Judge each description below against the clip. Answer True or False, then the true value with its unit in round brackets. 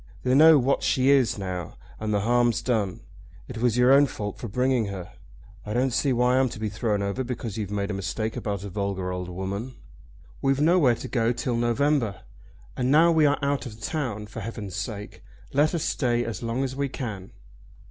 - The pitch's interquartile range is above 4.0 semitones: True (4.4 semitones)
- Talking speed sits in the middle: False (210 wpm)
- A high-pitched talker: False (120 Hz)